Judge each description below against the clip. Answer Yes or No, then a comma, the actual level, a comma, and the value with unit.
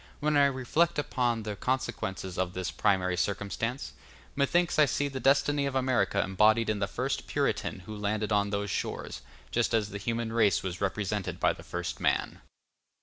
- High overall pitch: No, low, 110 Hz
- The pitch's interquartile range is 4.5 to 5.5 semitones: Yes, average, 4.9 semitones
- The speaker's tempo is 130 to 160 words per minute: No, average, 175 wpm